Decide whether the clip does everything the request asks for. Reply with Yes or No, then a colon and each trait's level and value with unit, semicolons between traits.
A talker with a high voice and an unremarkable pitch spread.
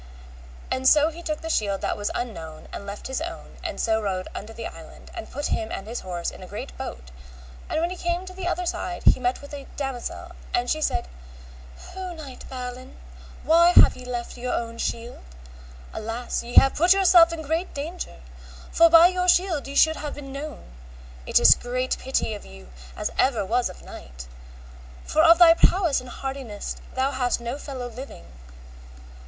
No: very high, 265 Hz; wide, 5.9 semitones